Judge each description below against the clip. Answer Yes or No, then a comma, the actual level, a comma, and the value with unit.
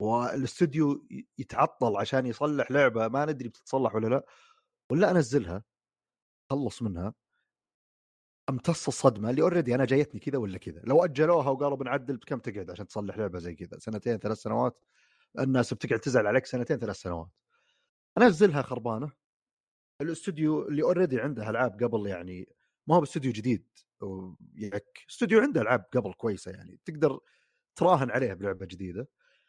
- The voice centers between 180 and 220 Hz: No, low, 130 Hz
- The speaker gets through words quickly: Yes, fast, 140 wpm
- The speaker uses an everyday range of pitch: No, wide, 5.8 semitones